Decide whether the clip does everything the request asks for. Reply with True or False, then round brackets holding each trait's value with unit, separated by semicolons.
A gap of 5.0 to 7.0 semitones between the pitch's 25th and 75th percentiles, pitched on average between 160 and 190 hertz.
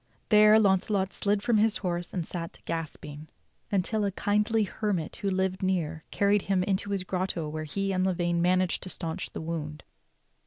False (3.2 semitones; 185 Hz)